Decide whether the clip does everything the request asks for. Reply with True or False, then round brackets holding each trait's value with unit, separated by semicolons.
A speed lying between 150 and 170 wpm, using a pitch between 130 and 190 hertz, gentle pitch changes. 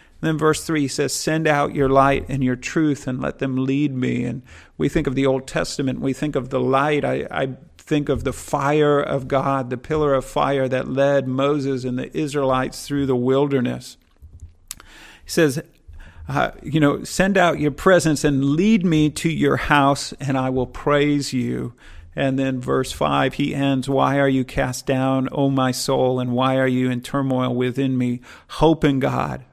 False (195 wpm; 135 Hz; 2.1 semitones)